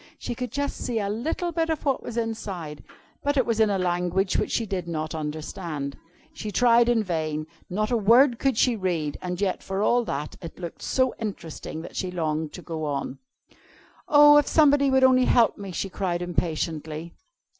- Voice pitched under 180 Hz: No, high, 195 Hz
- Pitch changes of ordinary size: No, wide, 6.6 semitones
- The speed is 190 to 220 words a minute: Yes, average, 195 wpm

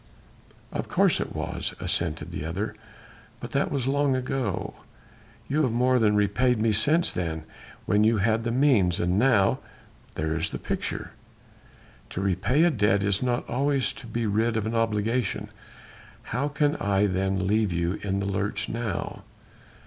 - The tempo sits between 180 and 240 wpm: No, average, 165 wpm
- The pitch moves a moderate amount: Yes, average, 4.4 semitones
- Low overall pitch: Yes, low, 110 Hz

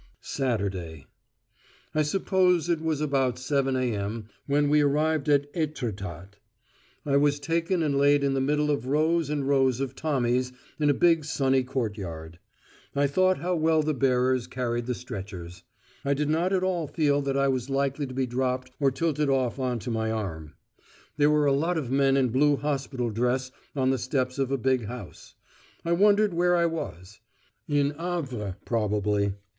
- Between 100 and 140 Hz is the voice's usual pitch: Yes, low, 135 Hz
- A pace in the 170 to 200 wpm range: Yes, average, 175 wpm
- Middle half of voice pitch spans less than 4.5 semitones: Yes, average, 3.5 semitones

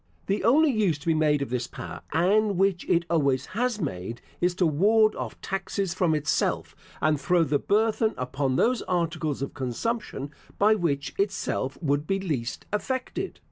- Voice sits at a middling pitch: Yes, medium, 170 Hz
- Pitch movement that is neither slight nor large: No, wide, 6.6 semitones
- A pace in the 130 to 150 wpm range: No, average, 170 wpm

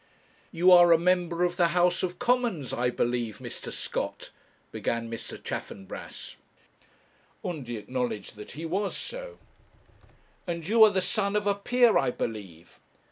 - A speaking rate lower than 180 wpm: Yes, average, 145 wpm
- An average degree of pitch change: No, wide, 8.4 semitones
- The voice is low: No, medium, 175 Hz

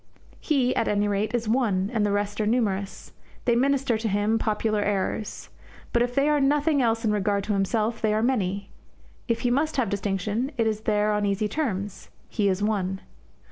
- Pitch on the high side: Yes, high, 215 Hz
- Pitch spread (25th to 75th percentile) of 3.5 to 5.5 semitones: No, average, 3.0 semitones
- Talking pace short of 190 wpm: No, average, 195 wpm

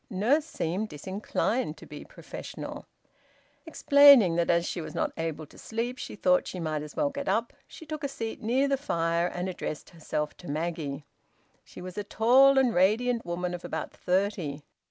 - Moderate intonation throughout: No, wide, 6.7 semitones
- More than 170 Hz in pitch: Yes, high, 190 Hz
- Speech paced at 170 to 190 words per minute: Yes, average, 180 wpm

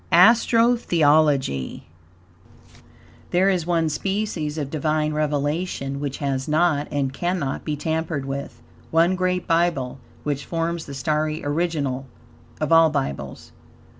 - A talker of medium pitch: Yes, medium, 155 Hz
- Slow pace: Yes, slow, 120 wpm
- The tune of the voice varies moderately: Yes, average, 3.2 semitones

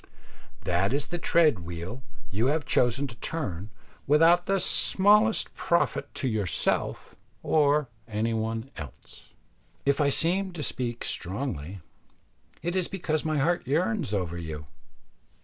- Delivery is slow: Yes, slow, 130 wpm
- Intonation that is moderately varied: No, wide, 8.1 semitones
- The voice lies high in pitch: No, low, 135 Hz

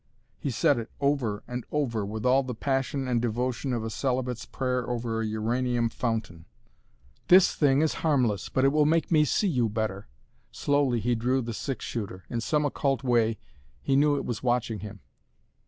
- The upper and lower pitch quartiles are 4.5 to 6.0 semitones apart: No, average, 3.4 semitones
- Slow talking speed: No, average, 185 wpm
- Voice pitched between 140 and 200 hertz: No, low, 125 Hz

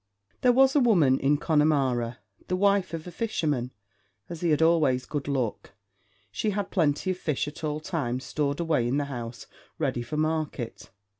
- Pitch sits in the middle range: Yes, medium, 150 Hz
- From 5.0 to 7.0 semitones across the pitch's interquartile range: No, average, 4.5 semitones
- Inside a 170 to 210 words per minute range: Yes, average, 175 wpm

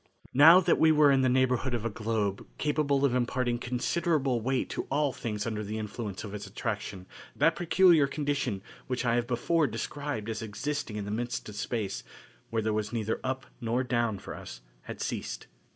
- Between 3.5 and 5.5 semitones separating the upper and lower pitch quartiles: Yes, average, 4.5 semitones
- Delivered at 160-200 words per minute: Yes, average, 190 wpm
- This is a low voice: Yes, low, 120 Hz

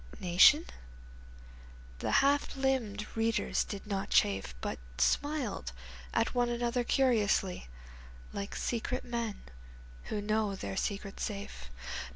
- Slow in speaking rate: Yes, slow, 110 wpm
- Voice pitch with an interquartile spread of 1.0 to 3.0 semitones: No, average, 3.7 semitones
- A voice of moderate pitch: No, high, 215 Hz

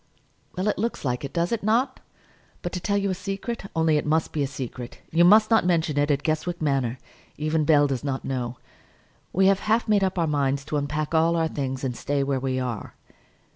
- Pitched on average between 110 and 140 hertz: No, medium, 155 Hz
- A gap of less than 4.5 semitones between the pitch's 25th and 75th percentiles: No, wide, 5.4 semitones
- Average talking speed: No, fast, 220 wpm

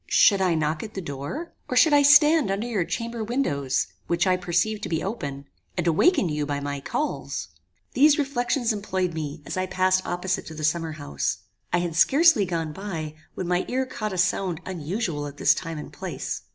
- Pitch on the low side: No, medium, 185 Hz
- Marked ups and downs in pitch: Yes, wide, 6.7 semitones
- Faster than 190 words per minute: Yes, average, 200 wpm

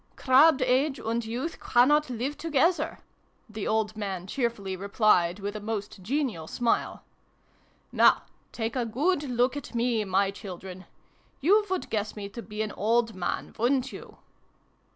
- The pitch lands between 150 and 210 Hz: No, high, 230 Hz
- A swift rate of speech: No, average, 165 wpm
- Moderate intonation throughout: Yes, average, 4.4 semitones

